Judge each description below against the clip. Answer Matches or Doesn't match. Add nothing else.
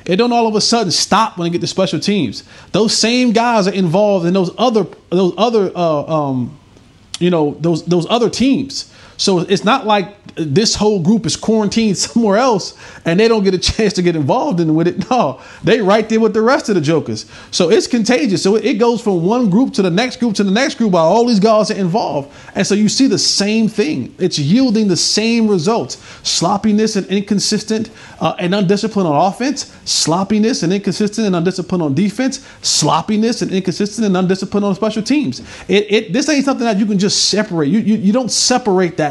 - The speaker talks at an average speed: Doesn't match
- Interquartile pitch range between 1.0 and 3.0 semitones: Doesn't match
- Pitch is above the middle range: Matches